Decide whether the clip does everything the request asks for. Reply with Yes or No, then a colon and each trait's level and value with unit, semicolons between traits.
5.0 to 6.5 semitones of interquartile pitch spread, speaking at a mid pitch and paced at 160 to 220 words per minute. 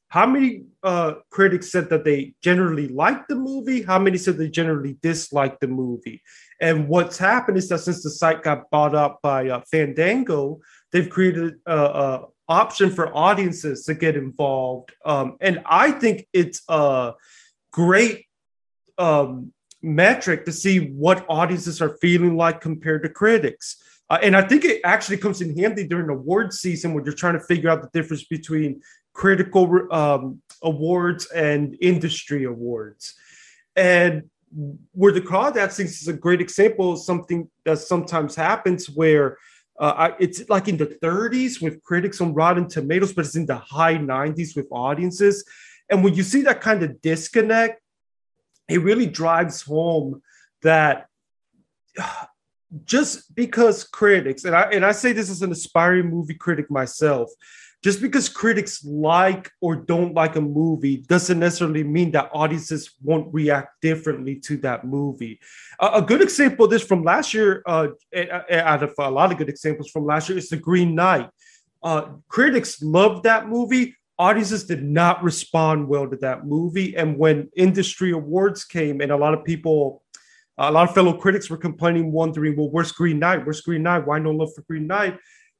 No: average, 4.1 semitones; medium, 170 Hz; average, 170 wpm